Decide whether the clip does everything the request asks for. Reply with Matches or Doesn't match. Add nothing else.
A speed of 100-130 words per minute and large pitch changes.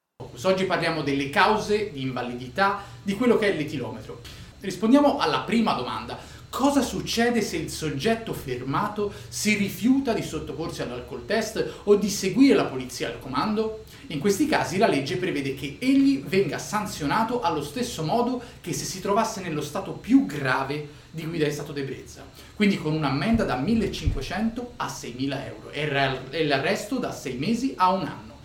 Doesn't match